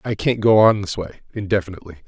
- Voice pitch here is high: No, low, 100 Hz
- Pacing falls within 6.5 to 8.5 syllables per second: Yes, 7.6 syllables/s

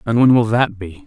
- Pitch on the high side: No, low, 110 Hz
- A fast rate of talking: Yes, fast, 280 wpm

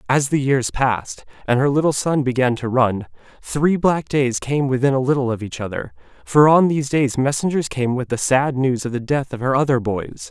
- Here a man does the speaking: Yes, male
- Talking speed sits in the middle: No, fast, 220 wpm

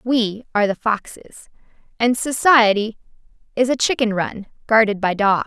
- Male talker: No, female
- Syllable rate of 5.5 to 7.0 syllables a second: No, 4.6 syllables/s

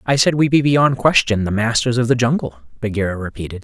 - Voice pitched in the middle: No, low, 120 Hz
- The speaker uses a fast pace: Yes, fast, 215 wpm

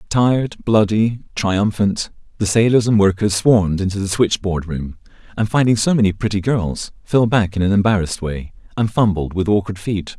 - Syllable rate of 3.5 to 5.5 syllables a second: Yes, 5.1 syllables/s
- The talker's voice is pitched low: Yes, low, 100 Hz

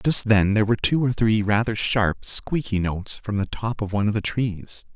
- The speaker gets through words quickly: Yes, fast, 230 wpm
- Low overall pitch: Yes, low, 110 Hz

